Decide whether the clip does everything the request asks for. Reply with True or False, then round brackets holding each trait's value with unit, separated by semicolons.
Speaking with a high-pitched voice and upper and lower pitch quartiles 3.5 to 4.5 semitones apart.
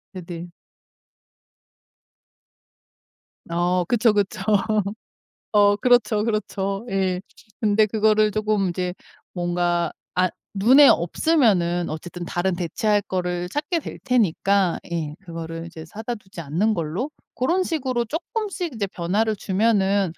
True (200 Hz; 4.0 semitones)